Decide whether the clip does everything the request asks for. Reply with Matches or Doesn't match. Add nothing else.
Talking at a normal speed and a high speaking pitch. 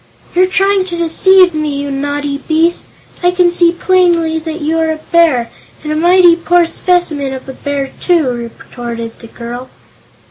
Matches